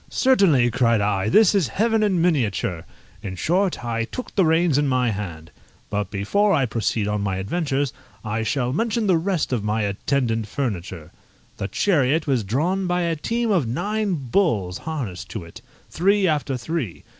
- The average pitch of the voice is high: No, low, 135 Hz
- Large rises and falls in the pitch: Yes, wide, 9.0 semitones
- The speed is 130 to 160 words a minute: No, average, 170 wpm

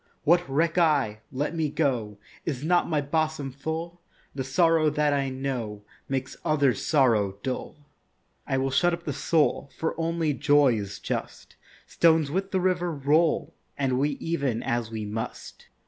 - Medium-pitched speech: Yes, medium, 145 Hz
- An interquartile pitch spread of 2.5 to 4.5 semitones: Yes, average, 3.7 semitones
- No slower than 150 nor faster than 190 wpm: Yes, average, 160 wpm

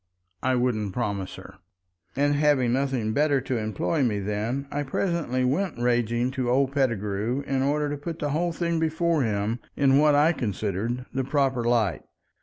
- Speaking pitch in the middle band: No, low, 130 Hz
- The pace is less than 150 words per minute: No, average, 160 wpm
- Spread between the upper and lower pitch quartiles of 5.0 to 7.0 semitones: No, average, 3.8 semitones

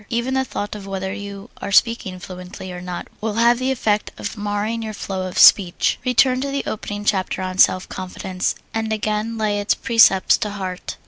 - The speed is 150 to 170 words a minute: No, average, 195 wpm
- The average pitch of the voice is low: No, high, 205 Hz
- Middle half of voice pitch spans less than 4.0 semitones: Yes, average, 3.1 semitones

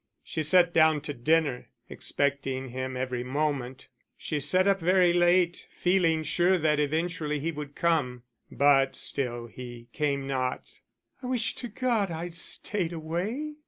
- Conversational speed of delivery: Yes, average, 145 wpm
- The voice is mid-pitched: Yes, medium, 155 Hz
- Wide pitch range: No, average, 4.5 semitones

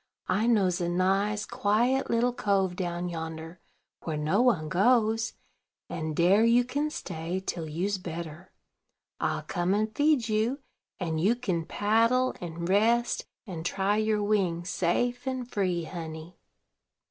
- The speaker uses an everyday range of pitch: Yes, average, 5.0 semitones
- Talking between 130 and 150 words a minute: Yes, average, 140 wpm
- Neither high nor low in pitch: No, high, 195 Hz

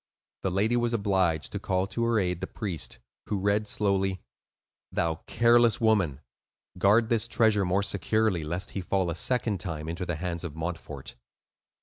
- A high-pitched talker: No, very low, 95 Hz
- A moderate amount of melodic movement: Yes, average, 4.0 semitones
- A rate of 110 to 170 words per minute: Yes, average, 165 wpm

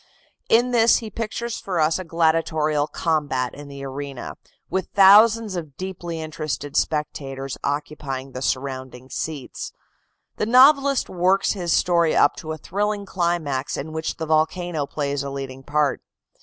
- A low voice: No, medium, 160 Hz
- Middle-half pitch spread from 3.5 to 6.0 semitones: Yes, average, 5.1 semitones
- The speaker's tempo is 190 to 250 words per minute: No, average, 145 wpm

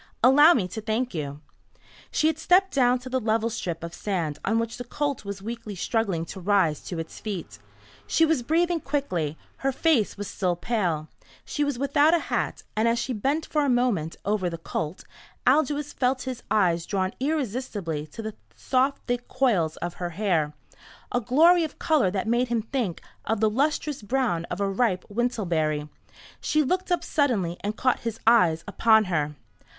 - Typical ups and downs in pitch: No, wide, 6.7 semitones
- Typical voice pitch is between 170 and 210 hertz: No, high, 225 Hz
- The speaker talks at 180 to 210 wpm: Yes, average, 185 wpm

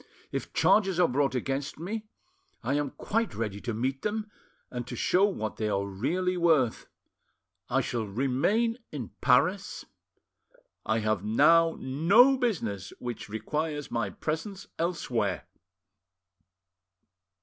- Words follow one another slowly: Yes, slow, 125 wpm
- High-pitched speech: No, medium, 140 Hz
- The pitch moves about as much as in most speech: No, wide, 8.3 semitones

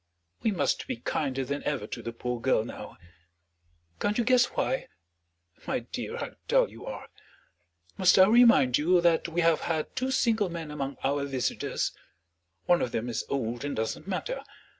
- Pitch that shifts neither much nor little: No, wide, 7.0 semitones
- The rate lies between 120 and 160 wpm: No, average, 175 wpm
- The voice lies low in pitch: No, medium, 150 Hz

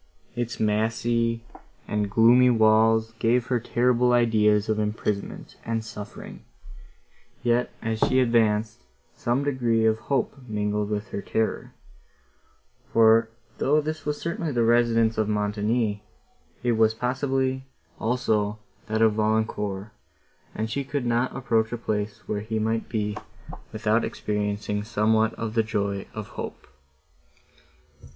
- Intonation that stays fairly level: Yes, narrow, 2.1 semitones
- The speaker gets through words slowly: Yes, slow, 130 wpm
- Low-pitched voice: Yes, low, 110 Hz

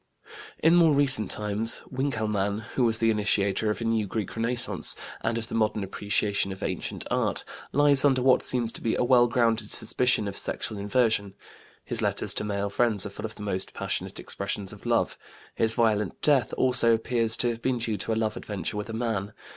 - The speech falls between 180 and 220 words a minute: Yes, average, 200 wpm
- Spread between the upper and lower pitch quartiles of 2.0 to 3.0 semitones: Yes, average, 2.7 semitones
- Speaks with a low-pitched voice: Yes, low, 110 Hz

